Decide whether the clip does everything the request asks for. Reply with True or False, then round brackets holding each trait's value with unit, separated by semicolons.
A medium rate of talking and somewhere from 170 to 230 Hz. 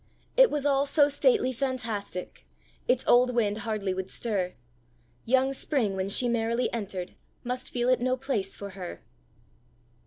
False (150 wpm; 240 Hz)